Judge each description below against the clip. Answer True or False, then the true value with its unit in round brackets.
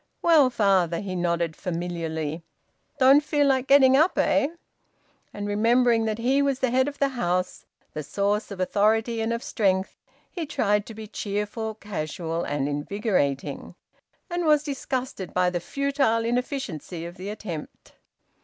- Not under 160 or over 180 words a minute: False (150 wpm)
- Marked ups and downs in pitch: True (6.5 semitones)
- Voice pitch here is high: True (215 Hz)